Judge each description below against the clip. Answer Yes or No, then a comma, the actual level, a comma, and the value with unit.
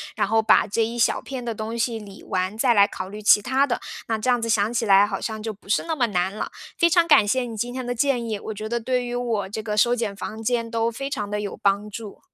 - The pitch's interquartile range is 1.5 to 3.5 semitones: Yes, average, 2.7 semitones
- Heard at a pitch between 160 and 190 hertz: No, high, 225 Hz